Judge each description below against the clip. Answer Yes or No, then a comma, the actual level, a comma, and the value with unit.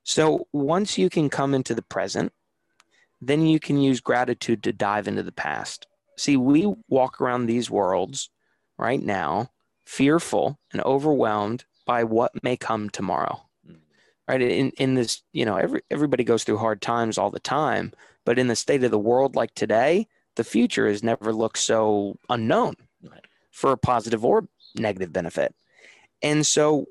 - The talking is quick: No, average, 165 wpm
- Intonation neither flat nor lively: Yes, average, 4.9 semitones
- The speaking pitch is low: Yes, low, 125 Hz